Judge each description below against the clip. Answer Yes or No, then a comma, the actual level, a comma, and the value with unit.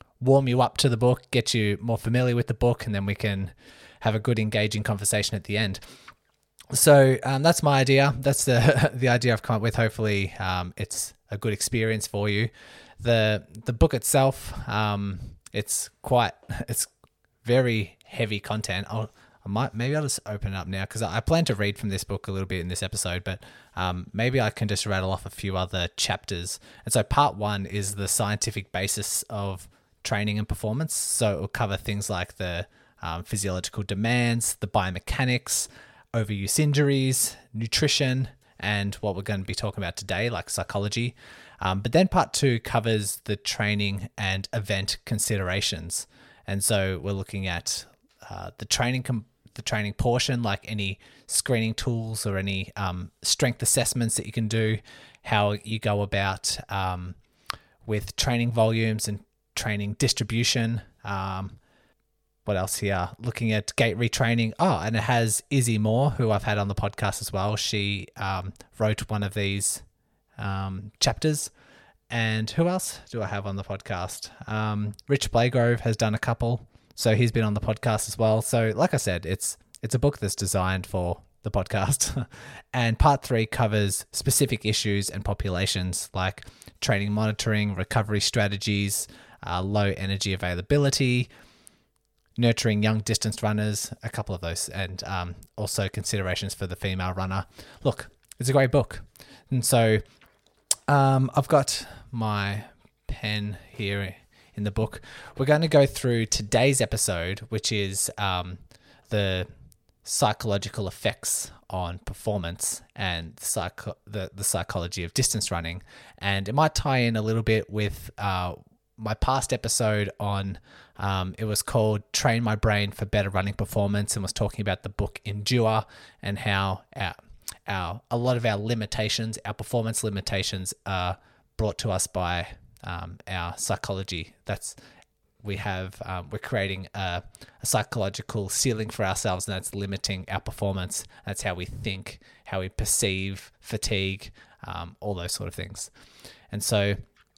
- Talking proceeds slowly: No, average, 165 wpm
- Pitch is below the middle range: Yes, low, 105 Hz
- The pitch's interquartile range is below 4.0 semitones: Yes, average, 3.0 semitones